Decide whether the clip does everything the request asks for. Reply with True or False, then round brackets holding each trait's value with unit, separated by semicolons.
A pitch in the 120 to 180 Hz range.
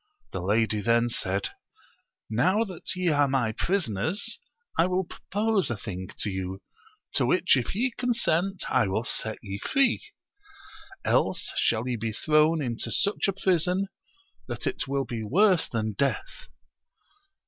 True (140 Hz)